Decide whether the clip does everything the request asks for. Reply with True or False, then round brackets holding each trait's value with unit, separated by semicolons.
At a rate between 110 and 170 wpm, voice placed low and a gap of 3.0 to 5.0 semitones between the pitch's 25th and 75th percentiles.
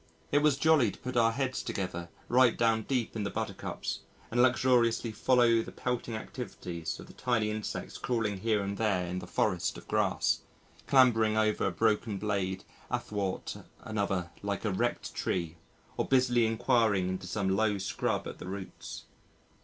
True (165 wpm; 110 Hz; 3.7 semitones)